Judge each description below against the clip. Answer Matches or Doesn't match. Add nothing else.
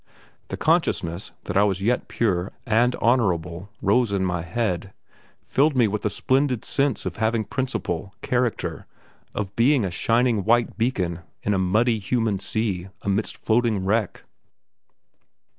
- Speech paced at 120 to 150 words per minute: Matches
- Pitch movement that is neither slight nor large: Matches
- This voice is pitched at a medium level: Doesn't match